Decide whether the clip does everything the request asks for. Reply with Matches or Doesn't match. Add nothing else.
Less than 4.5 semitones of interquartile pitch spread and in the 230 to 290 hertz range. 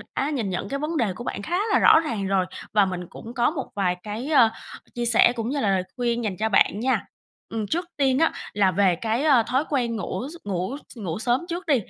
Doesn't match